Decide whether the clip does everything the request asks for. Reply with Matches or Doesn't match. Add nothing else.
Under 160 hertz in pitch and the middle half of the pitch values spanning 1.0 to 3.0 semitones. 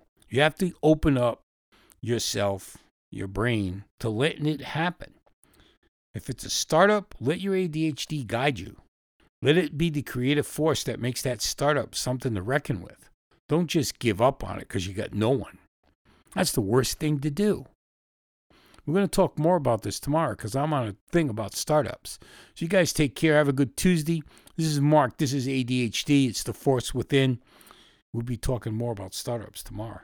Doesn't match